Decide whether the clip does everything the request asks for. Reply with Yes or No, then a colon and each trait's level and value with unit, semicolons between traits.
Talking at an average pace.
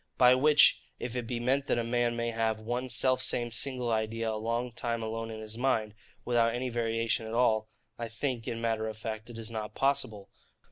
No: fast, 215 wpm